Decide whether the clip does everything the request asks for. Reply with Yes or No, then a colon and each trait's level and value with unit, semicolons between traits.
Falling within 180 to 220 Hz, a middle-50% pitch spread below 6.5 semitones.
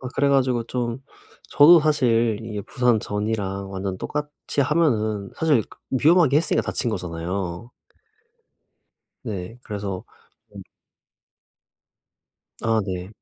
No: low, 115 Hz; wide, 5.6 semitones